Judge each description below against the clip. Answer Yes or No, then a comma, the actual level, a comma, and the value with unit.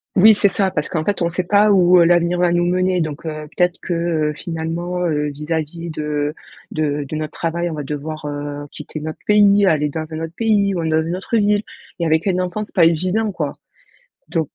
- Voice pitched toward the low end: No, medium, 170 Hz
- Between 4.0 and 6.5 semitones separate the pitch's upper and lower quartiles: No, average, 2.9 semitones